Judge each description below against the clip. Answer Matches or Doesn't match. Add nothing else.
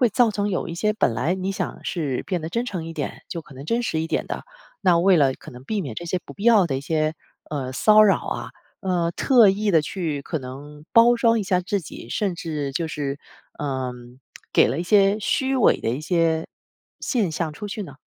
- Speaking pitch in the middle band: Matches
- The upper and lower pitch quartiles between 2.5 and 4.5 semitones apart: Doesn't match